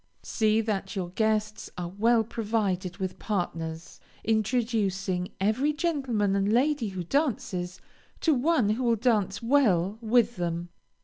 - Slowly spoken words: Yes, slow, 130 wpm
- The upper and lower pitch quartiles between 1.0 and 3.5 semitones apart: No, average, 4.0 semitones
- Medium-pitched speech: No, high, 215 Hz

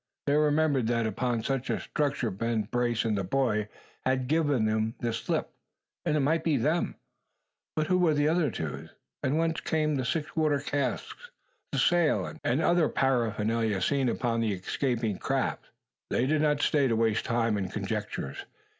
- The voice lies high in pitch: No, low, 130 Hz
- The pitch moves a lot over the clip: No, average, 5.0 semitones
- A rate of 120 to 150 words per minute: No, average, 170 wpm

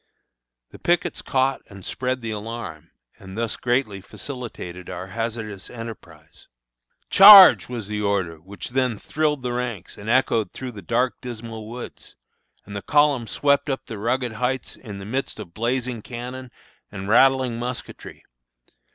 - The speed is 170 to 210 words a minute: No, average, 150 wpm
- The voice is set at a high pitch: No, low, 115 Hz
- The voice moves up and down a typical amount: Yes, average, 4.1 semitones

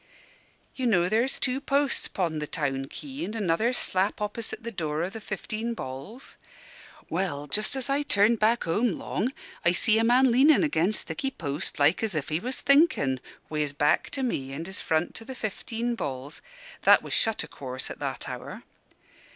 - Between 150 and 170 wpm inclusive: No, average, 190 wpm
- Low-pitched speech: No, high, 210 Hz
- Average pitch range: No, wide, 7.6 semitones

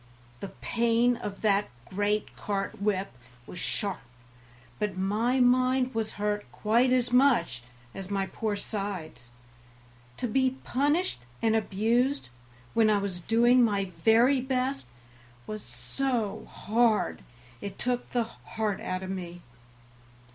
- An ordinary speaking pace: No, slow, 125 wpm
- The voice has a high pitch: Yes, high, 215 Hz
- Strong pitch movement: No, average, 3.9 semitones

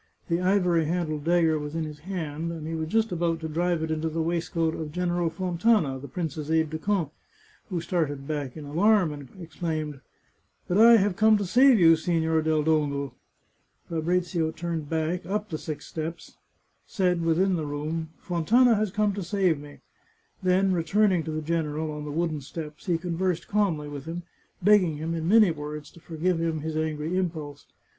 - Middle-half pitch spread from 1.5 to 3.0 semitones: Yes, narrow, 2.5 semitones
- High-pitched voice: No, medium, 165 Hz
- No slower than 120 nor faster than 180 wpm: No, average, 195 wpm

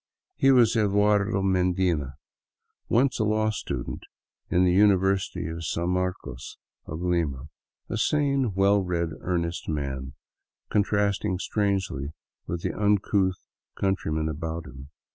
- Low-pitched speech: Yes, very low, 95 Hz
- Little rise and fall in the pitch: No, average, 3.8 semitones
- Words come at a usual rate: No, slow, 125 wpm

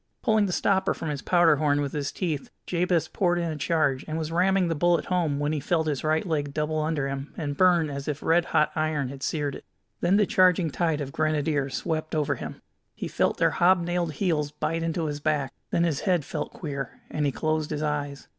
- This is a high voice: No, medium, 155 Hz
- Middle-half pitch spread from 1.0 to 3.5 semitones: Yes, average, 2.9 semitones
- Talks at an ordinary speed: No, fast, 220 wpm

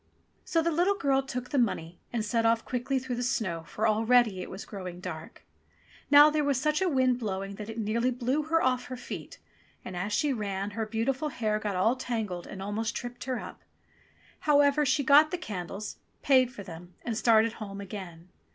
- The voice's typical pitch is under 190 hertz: No, high, 230 Hz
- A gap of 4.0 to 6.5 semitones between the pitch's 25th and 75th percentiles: Yes, average, 4.7 semitones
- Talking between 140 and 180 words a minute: No, average, 200 wpm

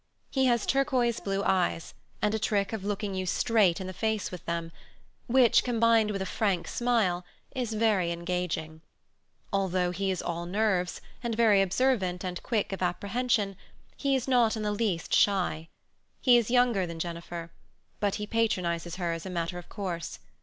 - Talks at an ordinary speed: Yes, average, 175 wpm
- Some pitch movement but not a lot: Yes, average, 4.3 semitones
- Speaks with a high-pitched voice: Yes, high, 195 Hz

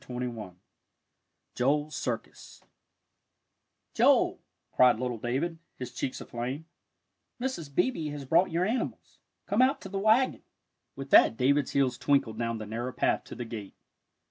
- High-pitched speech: No, low, 135 Hz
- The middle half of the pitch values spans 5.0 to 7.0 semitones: Yes, wide, 5.5 semitones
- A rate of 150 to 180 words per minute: No, average, 140 wpm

